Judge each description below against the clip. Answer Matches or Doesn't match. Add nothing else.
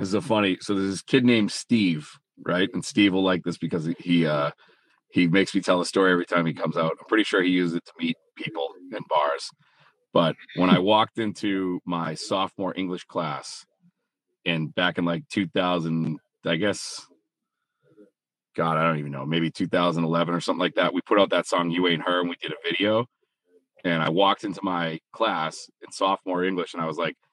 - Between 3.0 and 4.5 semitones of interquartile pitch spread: Doesn't match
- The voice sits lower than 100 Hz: Matches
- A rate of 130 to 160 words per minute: Doesn't match